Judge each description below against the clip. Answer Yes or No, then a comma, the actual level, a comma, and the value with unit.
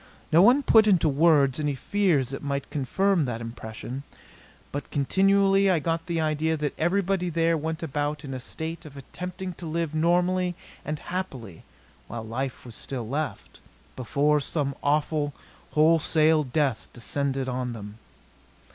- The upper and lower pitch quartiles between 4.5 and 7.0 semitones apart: No, average, 4.0 semitones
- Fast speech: No, average, 145 wpm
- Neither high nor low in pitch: Yes, medium, 150 Hz